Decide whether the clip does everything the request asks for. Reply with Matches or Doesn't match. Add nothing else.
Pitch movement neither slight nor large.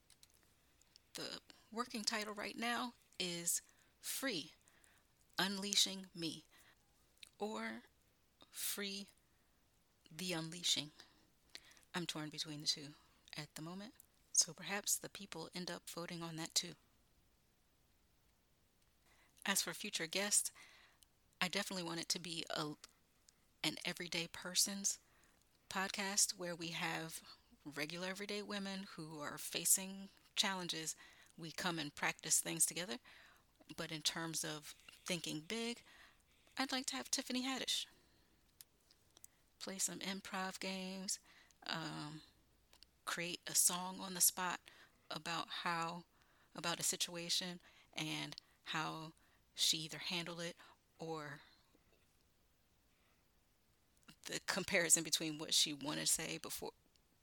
Matches